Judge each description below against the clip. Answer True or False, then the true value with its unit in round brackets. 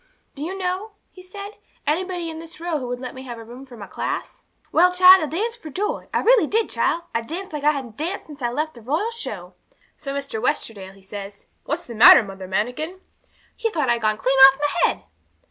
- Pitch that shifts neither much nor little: False (7.2 semitones)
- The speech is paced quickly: True (230 wpm)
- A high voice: True (295 Hz)